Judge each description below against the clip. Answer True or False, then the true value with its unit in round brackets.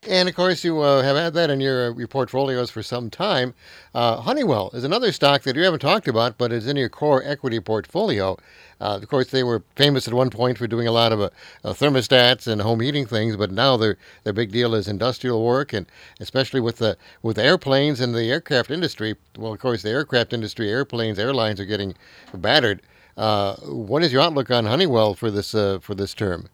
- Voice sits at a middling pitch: False (120 Hz)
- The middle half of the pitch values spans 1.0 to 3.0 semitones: False (3.8 semitones)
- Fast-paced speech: True (215 wpm)